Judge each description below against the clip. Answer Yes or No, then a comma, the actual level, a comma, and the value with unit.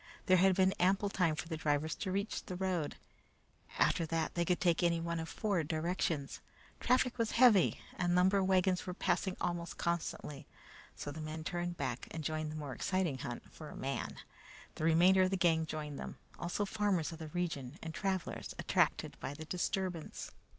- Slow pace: No, average, 185 wpm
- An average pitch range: Yes, average, 3.1 semitones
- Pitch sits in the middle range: Yes, medium, 170 Hz